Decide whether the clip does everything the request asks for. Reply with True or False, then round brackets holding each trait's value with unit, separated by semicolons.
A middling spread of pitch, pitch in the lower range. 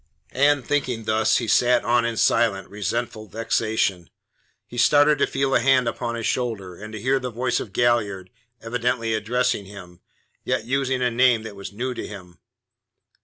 True (3.1 semitones; 115 Hz)